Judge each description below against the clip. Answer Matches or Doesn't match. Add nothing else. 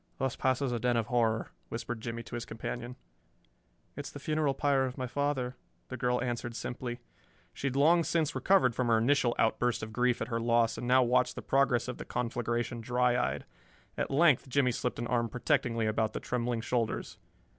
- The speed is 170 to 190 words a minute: Doesn't match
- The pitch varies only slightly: Matches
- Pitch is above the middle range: Doesn't match